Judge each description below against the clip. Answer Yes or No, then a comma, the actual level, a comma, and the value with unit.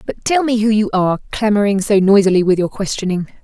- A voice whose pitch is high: Yes, high, 205 Hz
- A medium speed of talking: No, fast, 210 wpm